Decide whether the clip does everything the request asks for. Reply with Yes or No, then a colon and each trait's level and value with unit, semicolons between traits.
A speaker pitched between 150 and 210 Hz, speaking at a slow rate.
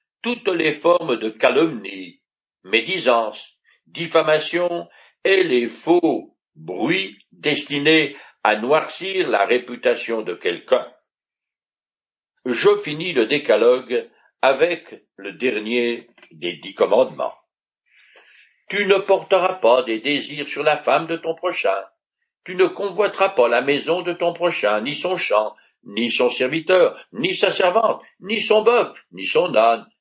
Yes: medium, 185 Hz; slow, 130 wpm